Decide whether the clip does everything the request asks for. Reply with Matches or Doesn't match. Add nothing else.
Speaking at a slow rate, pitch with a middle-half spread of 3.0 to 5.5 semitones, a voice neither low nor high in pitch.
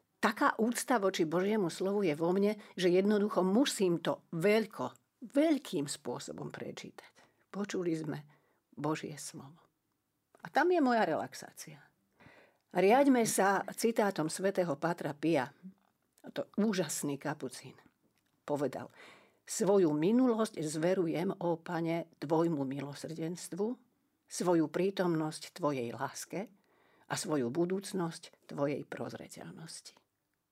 Matches